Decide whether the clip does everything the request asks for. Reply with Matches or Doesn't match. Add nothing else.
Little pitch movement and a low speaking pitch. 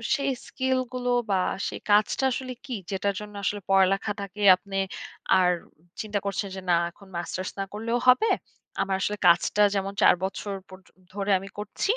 Doesn't match